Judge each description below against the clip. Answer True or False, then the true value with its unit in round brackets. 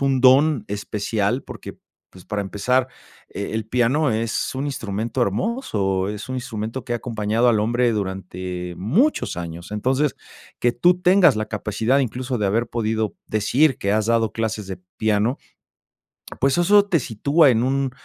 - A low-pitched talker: True (115 Hz)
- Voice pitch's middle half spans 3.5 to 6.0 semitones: True (4.1 semitones)